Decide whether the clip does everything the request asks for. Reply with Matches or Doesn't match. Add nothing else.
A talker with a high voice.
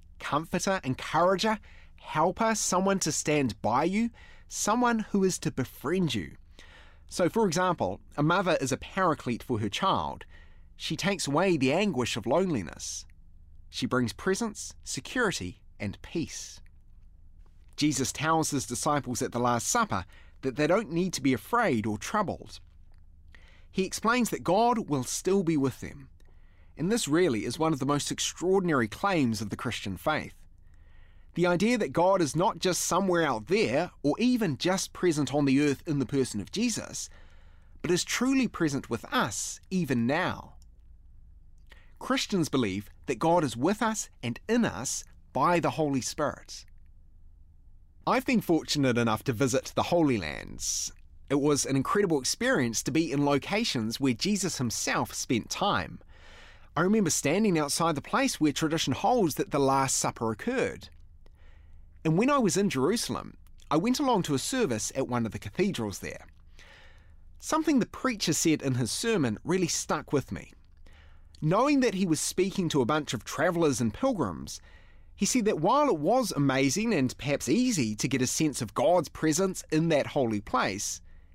Doesn't match